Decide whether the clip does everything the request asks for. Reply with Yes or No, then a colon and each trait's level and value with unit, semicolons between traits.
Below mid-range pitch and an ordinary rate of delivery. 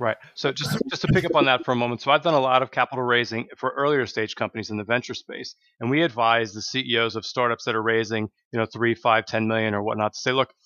No: low, 115 Hz; fast, 275 wpm